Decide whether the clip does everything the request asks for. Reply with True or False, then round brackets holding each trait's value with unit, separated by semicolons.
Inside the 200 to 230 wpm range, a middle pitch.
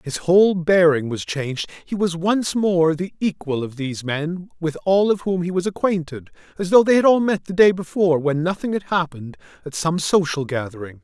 True (205 wpm; 170 Hz)